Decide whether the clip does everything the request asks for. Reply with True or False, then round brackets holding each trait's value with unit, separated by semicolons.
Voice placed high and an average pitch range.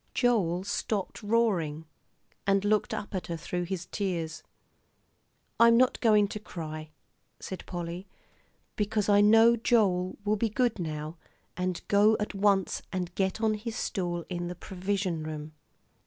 True (195 Hz; 3.4 semitones)